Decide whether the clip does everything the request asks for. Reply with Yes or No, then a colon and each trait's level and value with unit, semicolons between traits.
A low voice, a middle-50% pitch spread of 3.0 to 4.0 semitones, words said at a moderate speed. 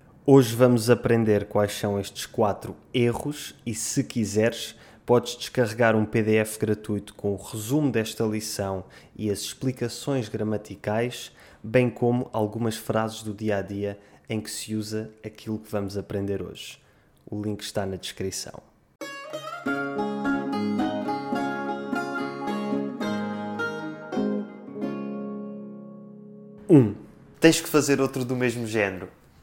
No: low, 110 Hz; average, 3.4 semitones; slow, 115 wpm